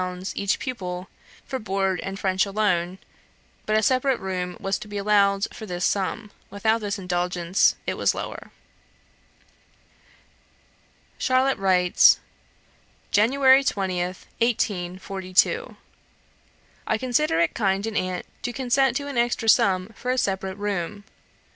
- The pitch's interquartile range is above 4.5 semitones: No, average, 4.1 semitones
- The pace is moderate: No, slow, 125 wpm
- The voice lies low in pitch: No, high, 200 Hz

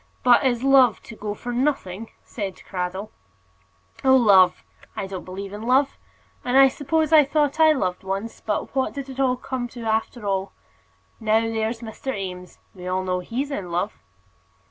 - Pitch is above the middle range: Yes, high, 225 Hz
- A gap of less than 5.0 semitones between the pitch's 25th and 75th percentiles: No, wide, 5.4 semitones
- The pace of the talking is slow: No, average, 165 wpm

